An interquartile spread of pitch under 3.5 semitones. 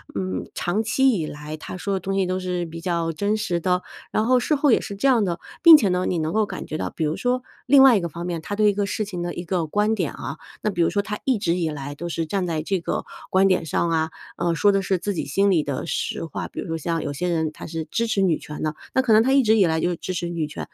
No: average, 4.1 semitones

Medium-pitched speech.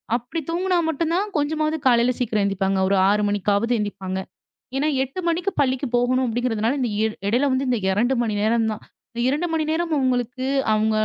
No: high, 245 Hz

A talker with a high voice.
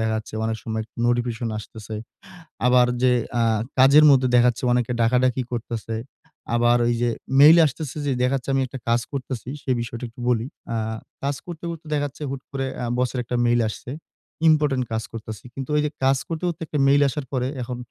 No: low, 125 Hz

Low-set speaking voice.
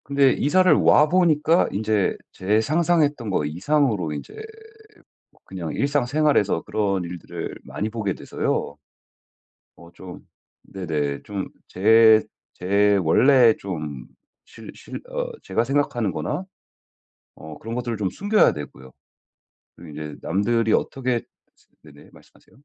Yes: low, 110 Hz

